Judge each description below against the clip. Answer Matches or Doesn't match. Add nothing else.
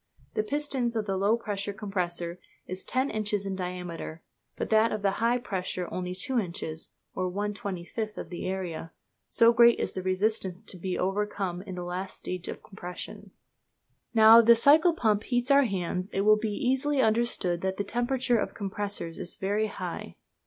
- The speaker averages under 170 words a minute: Doesn't match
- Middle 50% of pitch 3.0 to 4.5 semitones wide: Matches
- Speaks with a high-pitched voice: Matches